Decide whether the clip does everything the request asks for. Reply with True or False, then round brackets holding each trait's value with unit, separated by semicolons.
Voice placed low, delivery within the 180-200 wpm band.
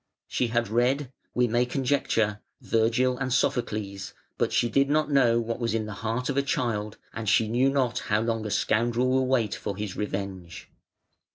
True (115 Hz; 185 wpm)